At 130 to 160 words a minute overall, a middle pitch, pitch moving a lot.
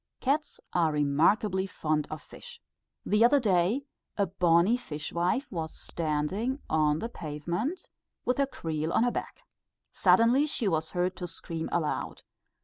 Yes: average, 140 wpm; medium, 180 Hz; wide, 6.9 semitones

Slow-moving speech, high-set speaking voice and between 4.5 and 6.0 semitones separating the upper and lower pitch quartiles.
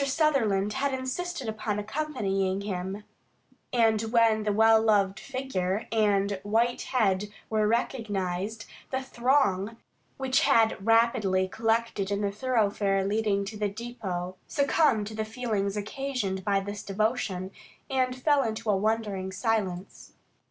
No: slow, 130 wpm; high, 215 Hz; average, 3.3 semitones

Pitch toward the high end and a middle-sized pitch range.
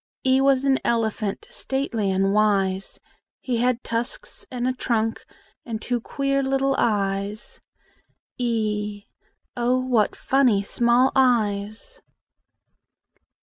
Yes: high, 235 Hz; average, 3.7 semitones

